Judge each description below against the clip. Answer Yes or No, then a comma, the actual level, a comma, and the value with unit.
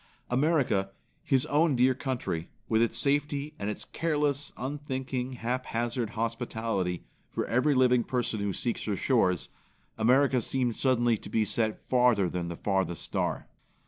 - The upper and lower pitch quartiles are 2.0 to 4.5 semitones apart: Yes, average, 3.2 semitones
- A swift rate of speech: No, average, 145 wpm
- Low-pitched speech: Yes, low, 125 Hz